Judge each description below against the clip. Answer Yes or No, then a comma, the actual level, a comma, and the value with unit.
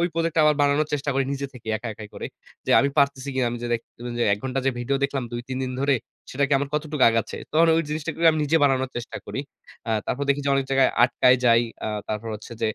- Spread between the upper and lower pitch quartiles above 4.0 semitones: No, average, 2.7 semitones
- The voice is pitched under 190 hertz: Yes, low, 135 Hz